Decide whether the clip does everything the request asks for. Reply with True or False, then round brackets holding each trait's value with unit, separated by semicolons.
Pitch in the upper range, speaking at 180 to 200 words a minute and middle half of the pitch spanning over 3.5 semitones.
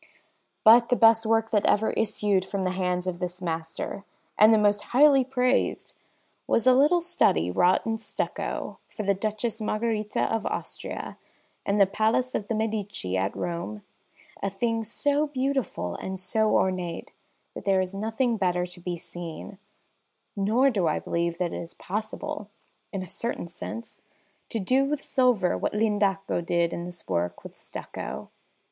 False (205 Hz; 165 wpm; 4.2 semitones)